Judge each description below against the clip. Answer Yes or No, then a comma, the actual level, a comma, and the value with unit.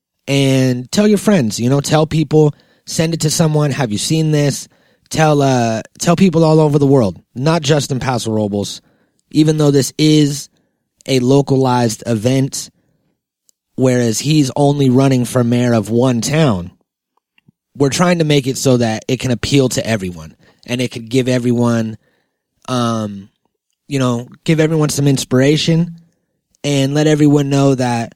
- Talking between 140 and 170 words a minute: Yes, average, 160 wpm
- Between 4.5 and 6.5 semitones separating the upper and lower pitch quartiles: No, average, 4.1 semitones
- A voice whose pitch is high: No, low, 135 Hz